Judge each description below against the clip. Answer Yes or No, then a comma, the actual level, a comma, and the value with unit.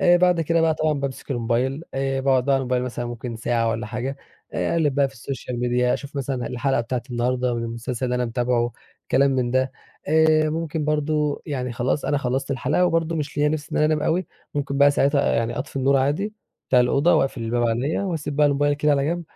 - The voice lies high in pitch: No, low, 135 Hz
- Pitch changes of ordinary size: Yes, average, 3.4 semitones